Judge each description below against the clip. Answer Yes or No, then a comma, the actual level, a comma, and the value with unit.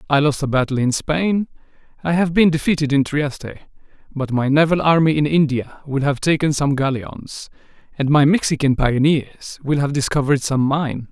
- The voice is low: No, medium, 145 Hz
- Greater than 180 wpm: No, average, 175 wpm